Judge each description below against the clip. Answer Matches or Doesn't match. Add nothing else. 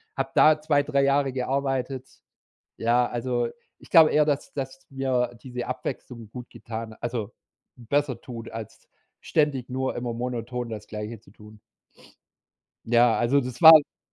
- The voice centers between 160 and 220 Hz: Doesn't match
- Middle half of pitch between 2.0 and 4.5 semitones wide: Matches